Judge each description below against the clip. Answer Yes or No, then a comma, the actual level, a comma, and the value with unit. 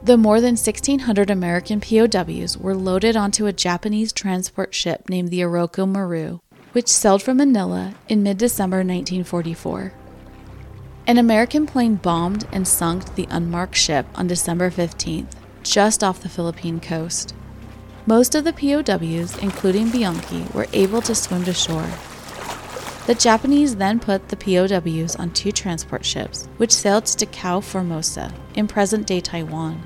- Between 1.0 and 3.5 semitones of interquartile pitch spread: No, average, 3.9 semitones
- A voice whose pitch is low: No, high, 190 Hz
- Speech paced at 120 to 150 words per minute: Yes, average, 145 wpm